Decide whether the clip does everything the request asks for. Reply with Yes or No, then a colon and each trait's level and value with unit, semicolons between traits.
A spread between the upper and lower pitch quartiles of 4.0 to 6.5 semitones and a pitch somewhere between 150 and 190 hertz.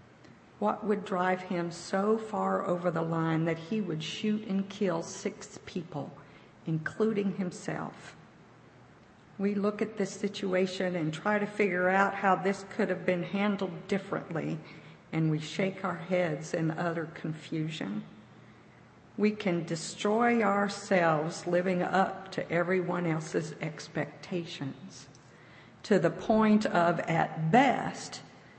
No: average, 3.3 semitones; medium, 185 Hz